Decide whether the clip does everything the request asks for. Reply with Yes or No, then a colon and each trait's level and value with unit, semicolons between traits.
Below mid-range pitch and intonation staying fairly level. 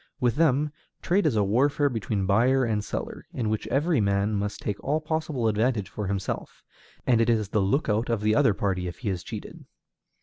No: low, 110 Hz; average, 4.8 semitones